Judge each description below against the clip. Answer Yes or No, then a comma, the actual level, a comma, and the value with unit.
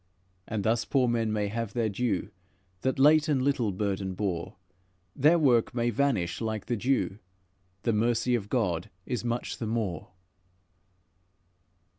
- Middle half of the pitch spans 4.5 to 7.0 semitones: No, average, 3.4 semitones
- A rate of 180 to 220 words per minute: No, average, 145 wpm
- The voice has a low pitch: Yes, low, 115 Hz